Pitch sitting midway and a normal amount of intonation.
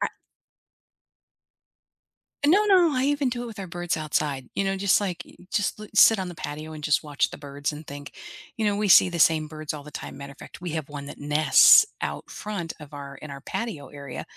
No: medium, 160 Hz; wide, 5.7 semitones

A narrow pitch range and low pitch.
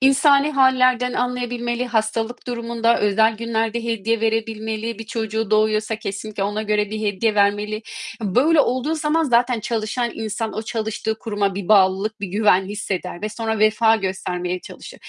No: narrow, 2.1 semitones; high, 220 Hz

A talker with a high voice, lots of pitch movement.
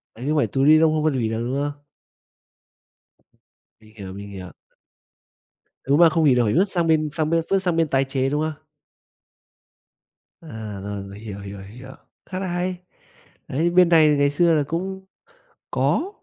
No: medium, 150 Hz; wide, 6.8 semitones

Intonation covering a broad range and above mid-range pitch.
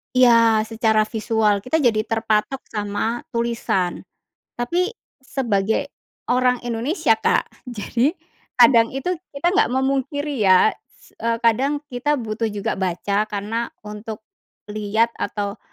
No: average, 3.0 semitones; high, 230 Hz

